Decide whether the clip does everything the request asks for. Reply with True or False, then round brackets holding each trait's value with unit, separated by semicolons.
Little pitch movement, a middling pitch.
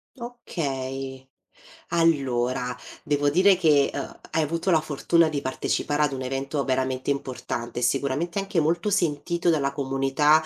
False (3.8 semitones; 145 Hz)